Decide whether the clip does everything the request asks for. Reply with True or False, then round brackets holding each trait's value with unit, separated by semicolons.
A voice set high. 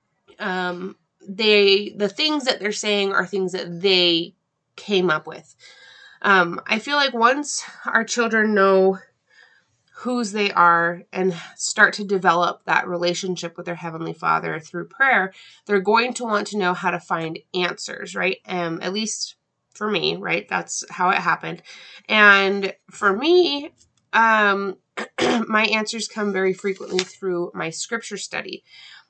True (195 Hz)